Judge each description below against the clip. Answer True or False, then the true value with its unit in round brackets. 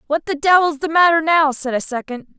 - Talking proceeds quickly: True (225 wpm)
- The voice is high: True (300 Hz)